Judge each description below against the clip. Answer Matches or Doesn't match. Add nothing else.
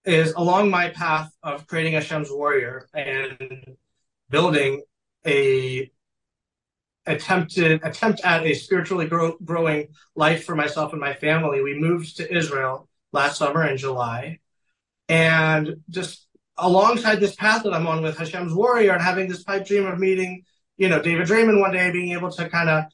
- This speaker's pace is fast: Doesn't match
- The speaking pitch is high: Doesn't match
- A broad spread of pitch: Doesn't match